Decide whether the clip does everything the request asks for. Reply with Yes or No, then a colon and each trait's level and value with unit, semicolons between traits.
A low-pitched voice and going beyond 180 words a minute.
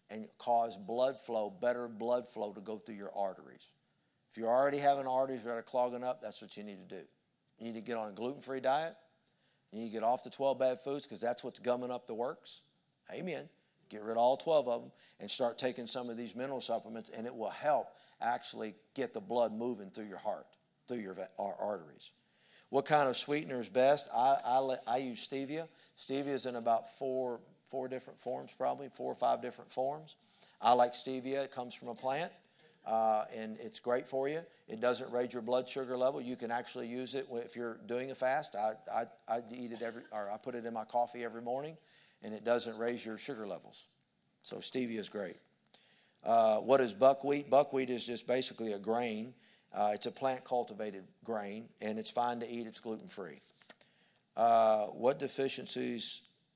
Yes: low, 120 Hz; fast, 205 wpm